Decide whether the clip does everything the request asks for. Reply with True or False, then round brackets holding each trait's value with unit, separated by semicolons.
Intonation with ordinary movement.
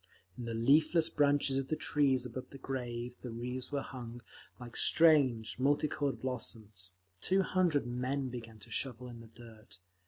True (3.2 semitones)